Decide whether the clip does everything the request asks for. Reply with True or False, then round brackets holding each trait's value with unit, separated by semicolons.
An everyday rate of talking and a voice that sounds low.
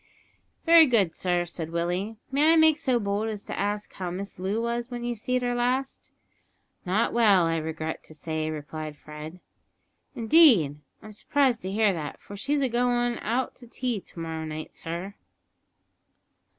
False (165 wpm; 205 Hz)